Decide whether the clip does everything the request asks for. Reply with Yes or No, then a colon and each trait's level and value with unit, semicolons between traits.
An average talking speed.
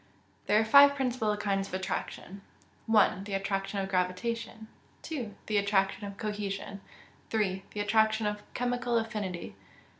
Yes: average, 150 wpm